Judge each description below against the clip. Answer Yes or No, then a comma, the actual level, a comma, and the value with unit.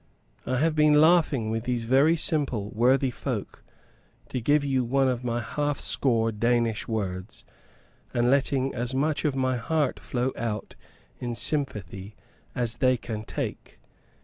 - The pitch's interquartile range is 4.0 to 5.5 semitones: No, average, 3.5 semitones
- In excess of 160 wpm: No, average, 145 wpm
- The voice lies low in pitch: Yes, low, 125 Hz